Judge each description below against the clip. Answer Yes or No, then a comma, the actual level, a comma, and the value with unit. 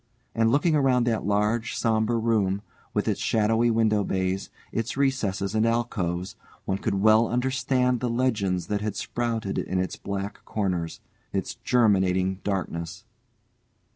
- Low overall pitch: Yes, low, 110 Hz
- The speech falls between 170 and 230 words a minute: No, average, 140 wpm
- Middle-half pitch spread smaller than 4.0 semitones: Yes, average, 3.5 semitones